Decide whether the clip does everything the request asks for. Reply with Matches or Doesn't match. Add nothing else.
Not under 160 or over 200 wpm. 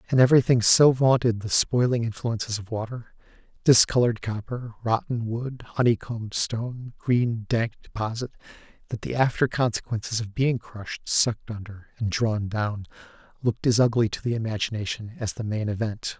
Doesn't match